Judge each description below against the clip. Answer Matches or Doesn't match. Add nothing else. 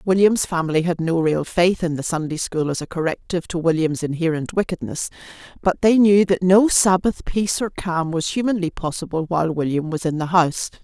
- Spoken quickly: Doesn't match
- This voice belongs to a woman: Matches